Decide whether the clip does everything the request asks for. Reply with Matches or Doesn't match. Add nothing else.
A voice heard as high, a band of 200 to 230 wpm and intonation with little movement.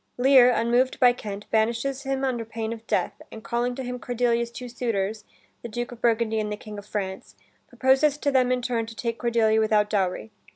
Matches